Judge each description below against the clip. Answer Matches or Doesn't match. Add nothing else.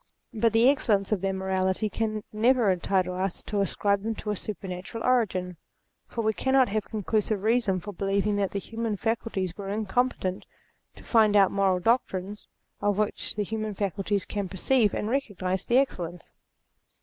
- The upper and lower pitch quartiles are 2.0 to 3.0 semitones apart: Matches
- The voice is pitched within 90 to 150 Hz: Doesn't match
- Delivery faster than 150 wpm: Matches